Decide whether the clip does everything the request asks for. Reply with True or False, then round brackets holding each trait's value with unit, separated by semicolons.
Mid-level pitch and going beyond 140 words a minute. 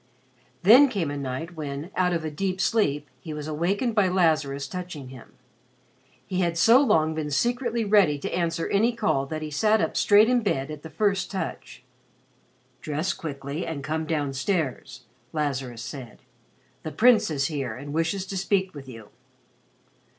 True (160 Hz; 170 wpm)